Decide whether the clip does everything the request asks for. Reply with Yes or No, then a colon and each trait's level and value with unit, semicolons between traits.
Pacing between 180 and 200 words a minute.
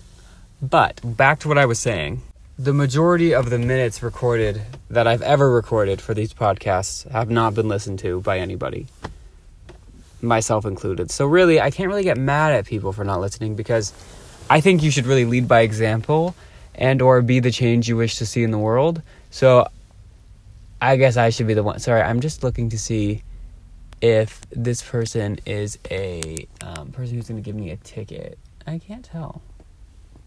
Yes: average, 185 wpm